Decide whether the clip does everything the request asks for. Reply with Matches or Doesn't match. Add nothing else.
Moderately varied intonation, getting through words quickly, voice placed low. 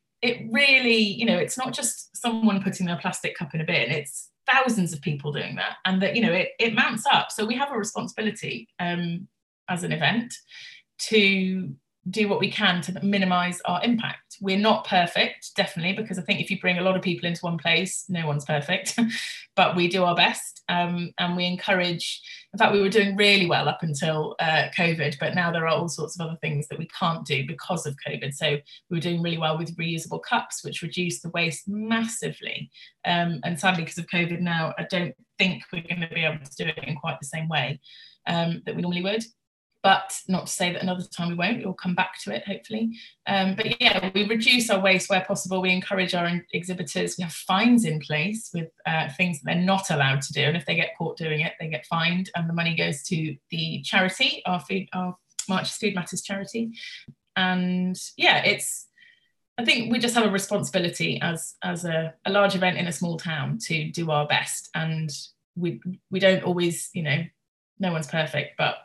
Doesn't match